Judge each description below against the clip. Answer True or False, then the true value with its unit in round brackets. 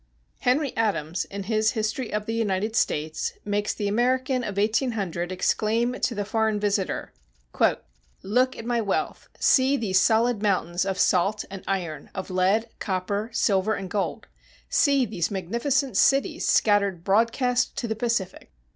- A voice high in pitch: True (210 Hz)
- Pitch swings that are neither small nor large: True (3.5 semitones)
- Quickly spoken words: False (145 wpm)